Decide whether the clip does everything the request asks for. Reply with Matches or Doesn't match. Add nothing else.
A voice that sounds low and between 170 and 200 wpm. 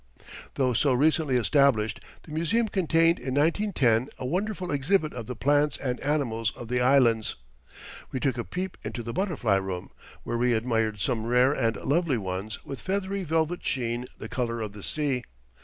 Matches